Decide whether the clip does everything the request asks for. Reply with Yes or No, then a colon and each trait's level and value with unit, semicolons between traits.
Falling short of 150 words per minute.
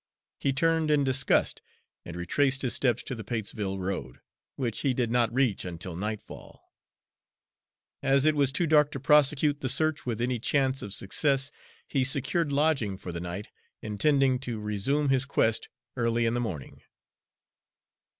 No: average, 160 wpm